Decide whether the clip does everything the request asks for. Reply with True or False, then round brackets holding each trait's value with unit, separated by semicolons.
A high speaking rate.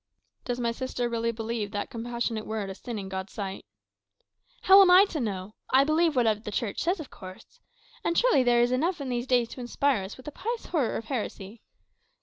True (210 wpm)